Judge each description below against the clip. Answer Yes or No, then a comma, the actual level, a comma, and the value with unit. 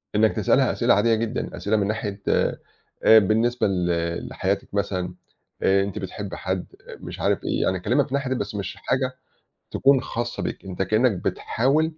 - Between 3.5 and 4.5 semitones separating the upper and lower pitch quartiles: Yes, average, 3.8 semitones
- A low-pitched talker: Yes, low, 105 Hz